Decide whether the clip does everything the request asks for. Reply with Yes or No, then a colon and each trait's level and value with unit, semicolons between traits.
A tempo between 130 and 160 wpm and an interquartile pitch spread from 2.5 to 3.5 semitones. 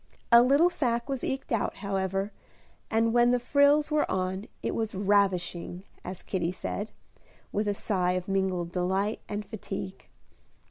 No: average, 150 wpm; average, 4.0 semitones